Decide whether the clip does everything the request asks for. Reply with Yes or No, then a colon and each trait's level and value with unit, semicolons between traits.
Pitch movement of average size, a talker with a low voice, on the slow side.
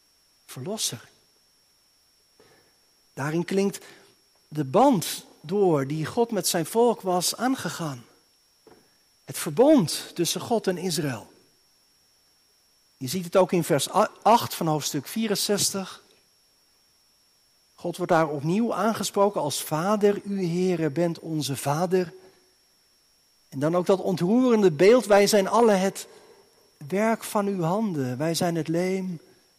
No: average, 4.6 semitones; medium, 185 Hz; slow, 120 wpm